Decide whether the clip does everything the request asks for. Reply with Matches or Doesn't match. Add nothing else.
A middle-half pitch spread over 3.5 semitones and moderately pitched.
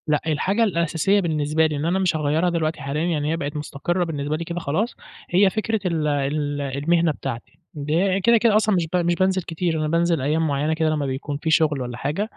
Doesn't match